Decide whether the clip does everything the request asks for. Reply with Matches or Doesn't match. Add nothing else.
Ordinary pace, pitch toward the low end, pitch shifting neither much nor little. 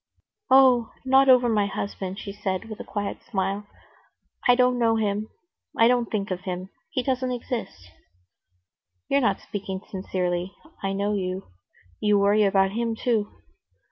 Doesn't match